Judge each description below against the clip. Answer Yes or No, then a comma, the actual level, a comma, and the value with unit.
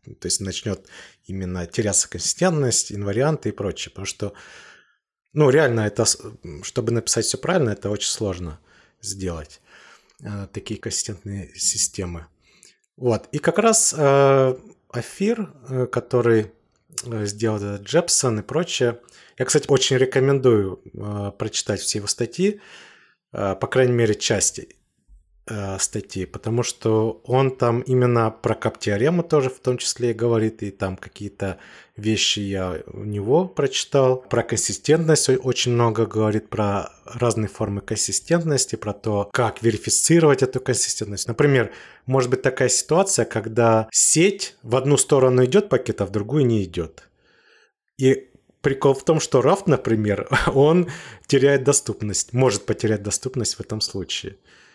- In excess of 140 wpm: No, average, 135 wpm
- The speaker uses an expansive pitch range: No, average, 4.4 semitones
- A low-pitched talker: Yes, low, 115 Hz